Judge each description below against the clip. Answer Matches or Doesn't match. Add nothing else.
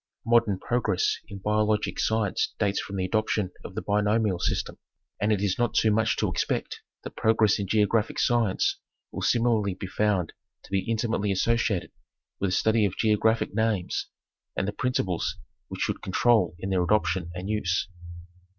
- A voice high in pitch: Doesn't match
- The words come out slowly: Doesn't match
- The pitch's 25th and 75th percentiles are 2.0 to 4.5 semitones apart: Matches